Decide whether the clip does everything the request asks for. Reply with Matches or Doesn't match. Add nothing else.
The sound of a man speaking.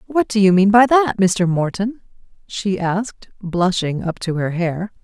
Doesn't match